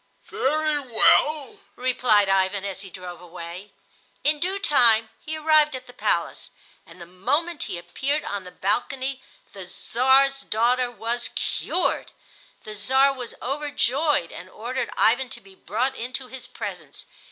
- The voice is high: Yes, high, 245 Hz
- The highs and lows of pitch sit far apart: Yes, wide, 5.8 semitones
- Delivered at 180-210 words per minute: No, average, 145 wpm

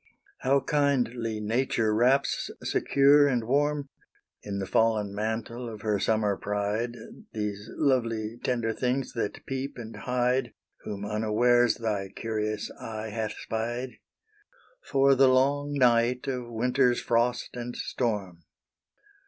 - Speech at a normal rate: No, slow, 120 wpm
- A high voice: No, low, 120 Hz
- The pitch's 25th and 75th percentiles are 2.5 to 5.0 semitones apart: Yes, average, 3.0 semitones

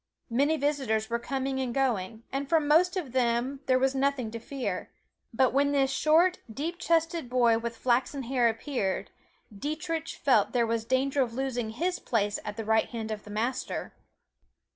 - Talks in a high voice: Yes, very high, 260 Hz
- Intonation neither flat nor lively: Yes, average, 3.6 semitones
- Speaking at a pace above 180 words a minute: No, average, 175 wpm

